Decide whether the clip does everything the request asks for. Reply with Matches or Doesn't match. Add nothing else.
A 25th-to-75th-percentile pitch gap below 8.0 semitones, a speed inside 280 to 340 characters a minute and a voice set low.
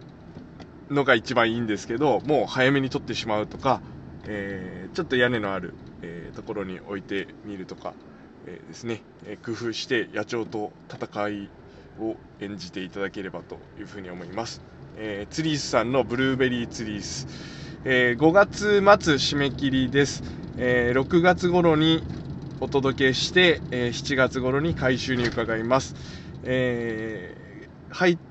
Matches